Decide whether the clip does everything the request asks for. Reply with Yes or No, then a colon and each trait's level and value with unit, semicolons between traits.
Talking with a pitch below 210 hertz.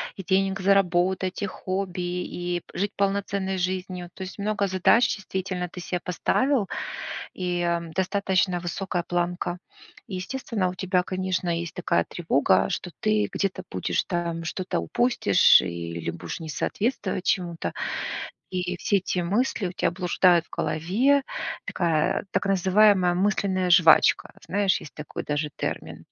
Yes: medium, 185 Hz